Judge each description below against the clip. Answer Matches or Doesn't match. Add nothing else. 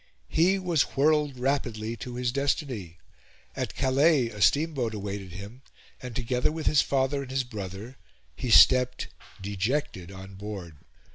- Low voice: Matches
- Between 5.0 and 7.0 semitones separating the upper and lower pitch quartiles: Matches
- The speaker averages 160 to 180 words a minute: Doesn't match